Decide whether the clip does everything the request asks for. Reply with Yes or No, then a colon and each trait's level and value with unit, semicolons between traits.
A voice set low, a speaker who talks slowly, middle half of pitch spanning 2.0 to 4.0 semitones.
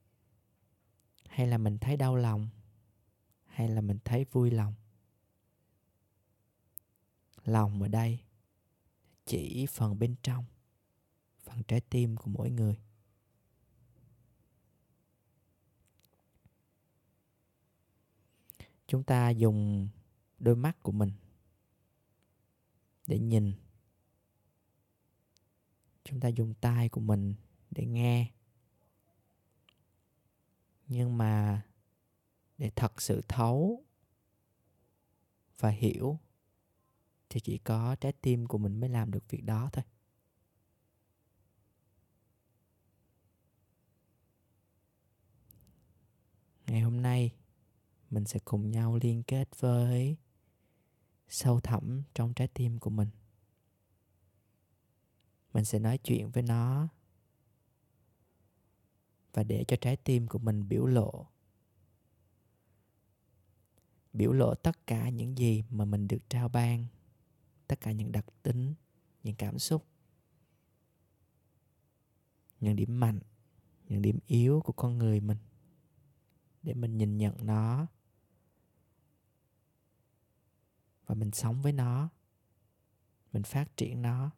Yes: low, 110 Hz; slow, 100 wpm; average, 2.9 semitones